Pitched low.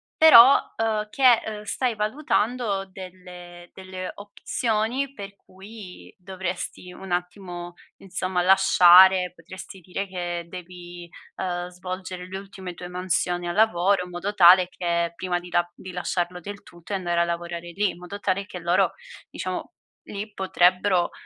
No: medium, 185 Hz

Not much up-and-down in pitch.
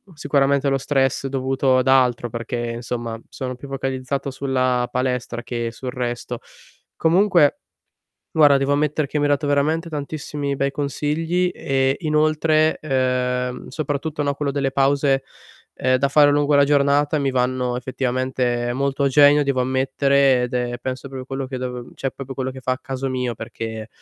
Yes: narrow, 2.0 semitones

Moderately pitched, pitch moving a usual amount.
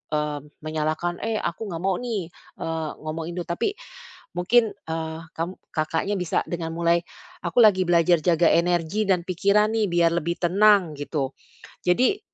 Yes: medium, 175 Hz; average, 3.2 semitones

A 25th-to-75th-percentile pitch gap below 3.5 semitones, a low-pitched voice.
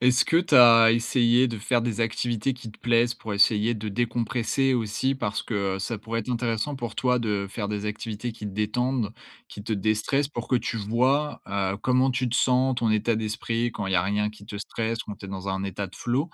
Yes: average, 2.9 semitones; low, 115 Hz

